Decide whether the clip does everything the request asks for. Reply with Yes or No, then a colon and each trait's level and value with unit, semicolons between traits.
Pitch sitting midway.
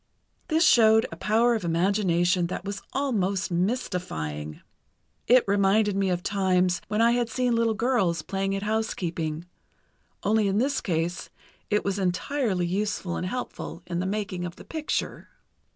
No: high, 195 Hz